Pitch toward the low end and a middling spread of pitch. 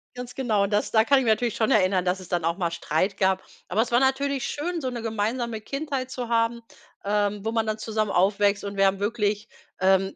No: high, 215 Hz; average, 3.4 semitones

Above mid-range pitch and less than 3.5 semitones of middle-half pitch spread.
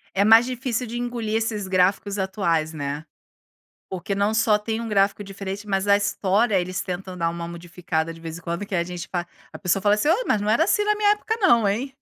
No: high, 200 Hz; average, 3.9 semitones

